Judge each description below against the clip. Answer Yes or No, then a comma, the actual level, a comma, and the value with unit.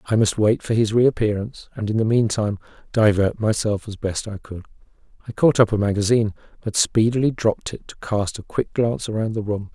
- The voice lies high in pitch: No, low, 110 Hz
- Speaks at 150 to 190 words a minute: No, fast, 205 wpm